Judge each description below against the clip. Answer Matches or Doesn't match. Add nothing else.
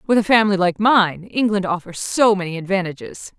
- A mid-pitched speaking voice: Doesn't match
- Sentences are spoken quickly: Doesn't match